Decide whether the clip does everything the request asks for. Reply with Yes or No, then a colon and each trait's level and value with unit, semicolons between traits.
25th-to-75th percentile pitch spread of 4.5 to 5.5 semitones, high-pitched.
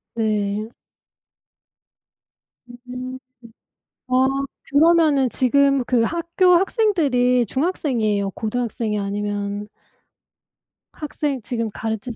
Yes: average, 5.1 semitones; very high, 250 Hz